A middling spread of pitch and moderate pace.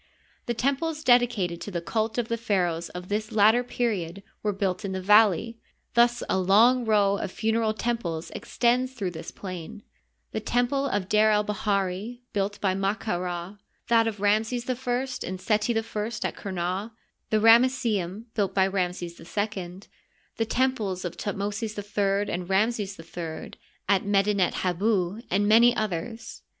Yes: average, 3.5 semitones; average, 160 wpm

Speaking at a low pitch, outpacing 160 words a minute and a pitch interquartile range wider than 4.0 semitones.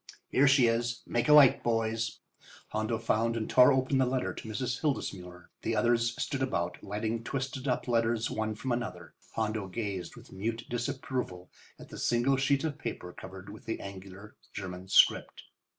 No: low, 115 Hz; average, 170 wpm; average, 3.4 semitones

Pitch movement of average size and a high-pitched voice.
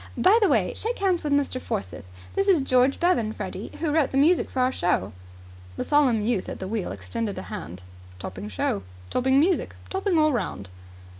No: wide, 8.8 semitones; very high, 260 Hz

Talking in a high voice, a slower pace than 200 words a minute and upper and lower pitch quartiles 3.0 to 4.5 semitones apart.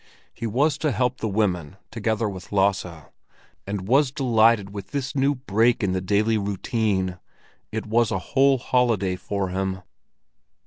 No: low, 110 Hz; average, 145 wpm; average, 4.2 semitones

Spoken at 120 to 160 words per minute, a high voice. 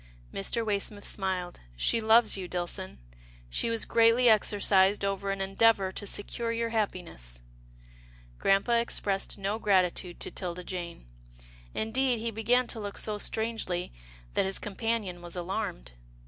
Yes: average, 145 wpm; high, 200 Hz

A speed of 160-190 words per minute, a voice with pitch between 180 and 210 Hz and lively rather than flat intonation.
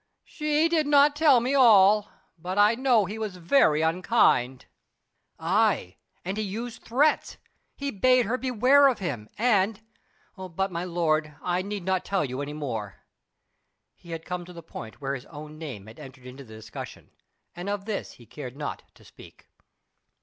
Yes: average, 170 wpm; medium, 185 Hz; wide, 7.2 semitones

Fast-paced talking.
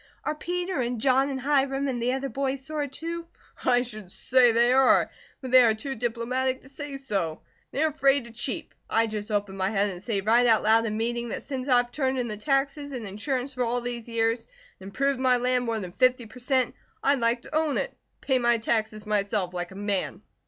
Yes: fast, 225 wpm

